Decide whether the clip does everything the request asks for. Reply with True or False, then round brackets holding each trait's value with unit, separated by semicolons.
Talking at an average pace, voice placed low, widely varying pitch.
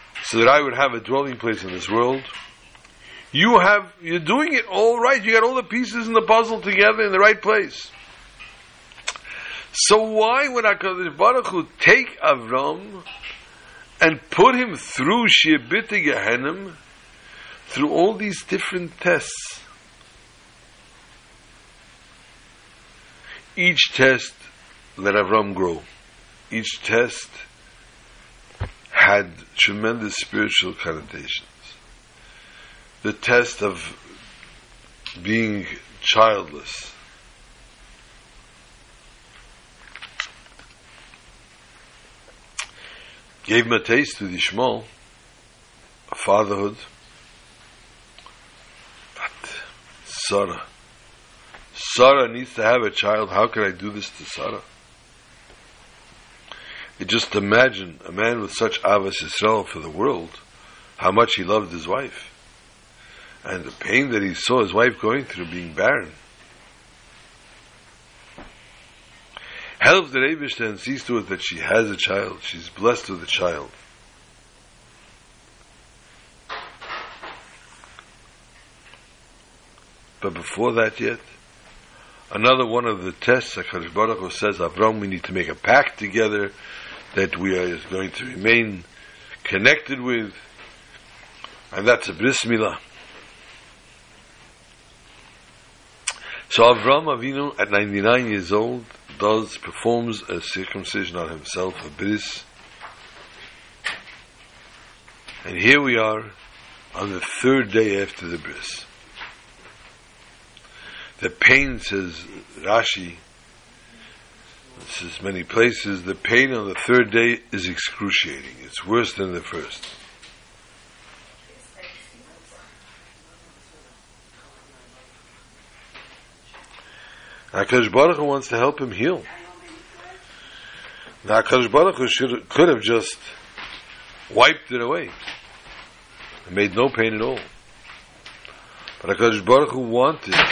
False (100 wpm; 115 Hz; 6.2 semitones)